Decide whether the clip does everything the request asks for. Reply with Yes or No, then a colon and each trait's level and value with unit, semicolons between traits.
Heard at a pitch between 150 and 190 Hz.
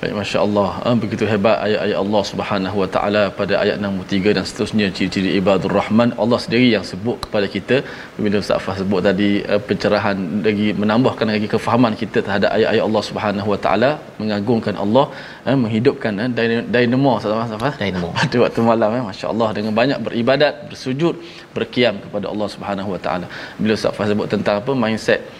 No: low, 105 Hz